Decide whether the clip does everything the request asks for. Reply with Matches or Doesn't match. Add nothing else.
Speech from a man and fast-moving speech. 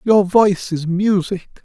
Doesn't match